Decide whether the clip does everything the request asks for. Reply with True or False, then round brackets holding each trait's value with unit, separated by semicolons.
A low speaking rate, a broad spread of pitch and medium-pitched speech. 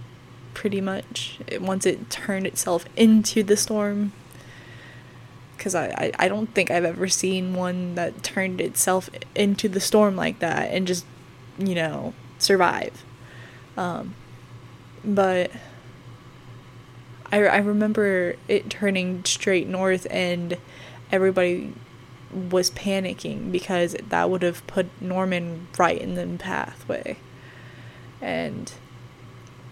True (115 wpm; 7.3 semitones; 175 Hz)